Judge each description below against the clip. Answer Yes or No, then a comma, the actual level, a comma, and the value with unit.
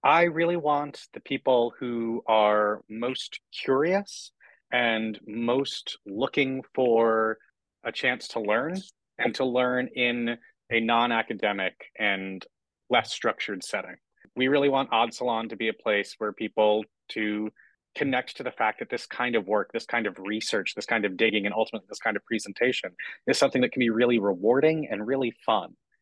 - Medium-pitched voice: No, low, 115 Hz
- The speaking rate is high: No, average, 165 wpm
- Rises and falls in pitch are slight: No, average, 3.1 semitones